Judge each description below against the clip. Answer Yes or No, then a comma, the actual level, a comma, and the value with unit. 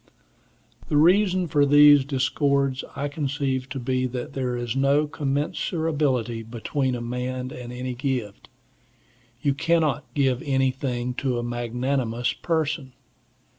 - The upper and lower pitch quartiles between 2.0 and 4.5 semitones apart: Yes, average, 2.7 semitones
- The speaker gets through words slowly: Yes, slow, 125 wpm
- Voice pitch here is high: No, low, 135 Hz